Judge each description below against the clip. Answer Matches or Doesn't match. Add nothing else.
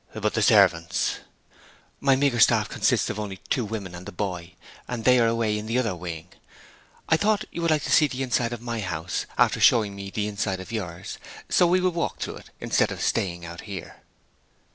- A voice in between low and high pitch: Doesn't match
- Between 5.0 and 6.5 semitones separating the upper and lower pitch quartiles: Matches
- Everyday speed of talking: Doesn't match